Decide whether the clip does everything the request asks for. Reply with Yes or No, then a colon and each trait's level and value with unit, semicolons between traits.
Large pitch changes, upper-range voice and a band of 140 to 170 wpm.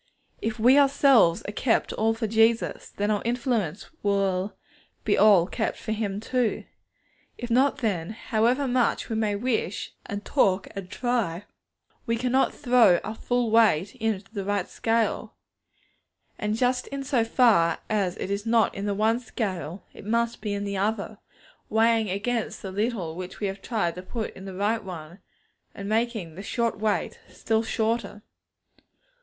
No: average, 2.9 semitones; high, 220 Hz; average, 165 wpm